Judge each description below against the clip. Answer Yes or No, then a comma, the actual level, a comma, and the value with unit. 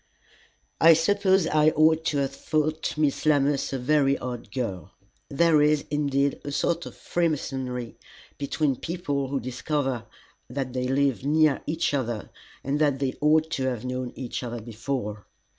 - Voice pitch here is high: No, medium, 140 Hz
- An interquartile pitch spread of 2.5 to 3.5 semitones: Yes, average, 3.2 semitones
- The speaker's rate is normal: Yes, average, 155 wpm